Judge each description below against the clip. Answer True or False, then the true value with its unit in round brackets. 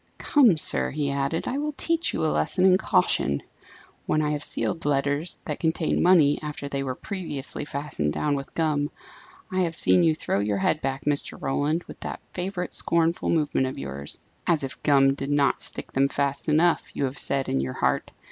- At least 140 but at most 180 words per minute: False (195 wpm)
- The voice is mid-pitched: True (145 Hz)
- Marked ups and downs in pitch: False (3.4 semitones)